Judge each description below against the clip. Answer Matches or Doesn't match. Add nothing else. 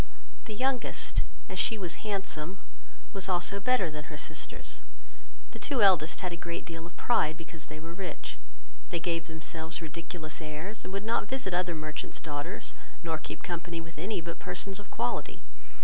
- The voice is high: Doesn't match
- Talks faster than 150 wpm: Matches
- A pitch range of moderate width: Matches